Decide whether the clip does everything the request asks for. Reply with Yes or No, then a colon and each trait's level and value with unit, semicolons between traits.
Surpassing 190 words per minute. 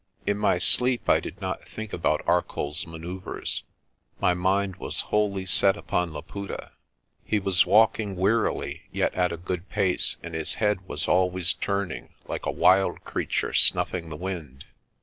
No: average, 155 wpm